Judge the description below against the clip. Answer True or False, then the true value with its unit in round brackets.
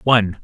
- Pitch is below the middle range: True (110 Hz)